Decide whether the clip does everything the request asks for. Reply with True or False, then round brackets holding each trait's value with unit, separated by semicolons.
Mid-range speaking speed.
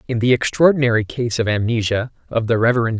True (180 wpm)